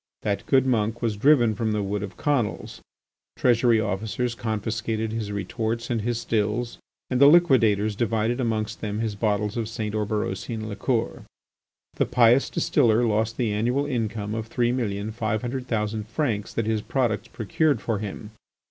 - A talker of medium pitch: No, low, 110 Hz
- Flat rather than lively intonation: Yes, narrow, 2.2 semitones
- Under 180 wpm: Yes, average, 160 wpm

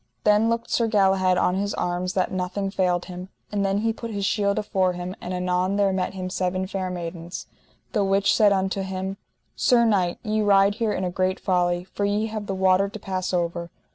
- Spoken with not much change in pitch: Yes, narrow, 1.9 semitones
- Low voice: No, high, 190 Hz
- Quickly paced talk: Yes, fast, 210 wpm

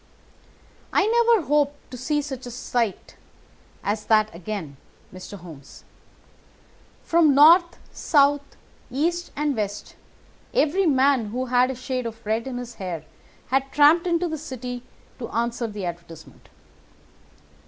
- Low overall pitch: No, very high, 255 Hz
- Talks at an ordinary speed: No, slow, 130 wpm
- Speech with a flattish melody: No, wide, 5.4 semitones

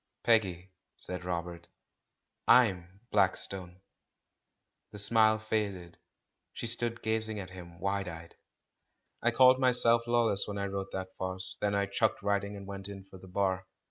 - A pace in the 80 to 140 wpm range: No, average, 150 wpm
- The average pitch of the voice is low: Yes, low, 100 Hz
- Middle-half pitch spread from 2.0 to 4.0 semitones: Yes, average, 2.9 semitones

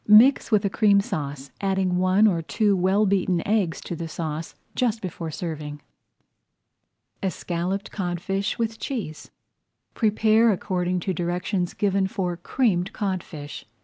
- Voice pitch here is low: No, medium, 185 Hz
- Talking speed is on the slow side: Yes, slow, 130 wpm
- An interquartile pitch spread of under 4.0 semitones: Yes, average, 3.1 semitones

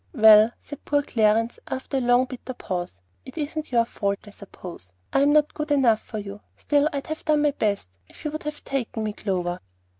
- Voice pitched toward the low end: No, high, 240 Hz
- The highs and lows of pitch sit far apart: Yes, wide, 5.7 semitones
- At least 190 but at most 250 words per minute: Yes, fast, 205 wpm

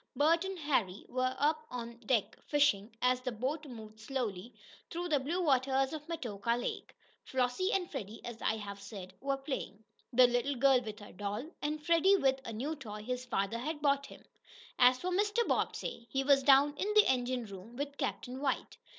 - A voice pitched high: Yes, very high, 260 Hz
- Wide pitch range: No, average, 4.1 semitones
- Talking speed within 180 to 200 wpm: Yes, average, 190 wpm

